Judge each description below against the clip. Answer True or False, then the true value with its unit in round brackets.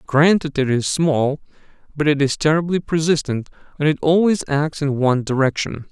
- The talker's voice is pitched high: False (150 Hz)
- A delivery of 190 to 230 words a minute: False (160 wpm)